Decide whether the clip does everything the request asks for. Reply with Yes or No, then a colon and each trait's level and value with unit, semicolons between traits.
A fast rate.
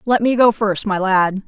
Yes: fast, 245 wpm